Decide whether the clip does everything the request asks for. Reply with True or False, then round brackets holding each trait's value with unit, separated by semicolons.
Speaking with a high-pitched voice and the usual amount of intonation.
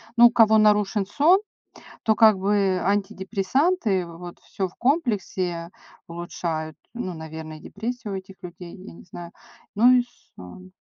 True (195 Hz; 4.1 semitones)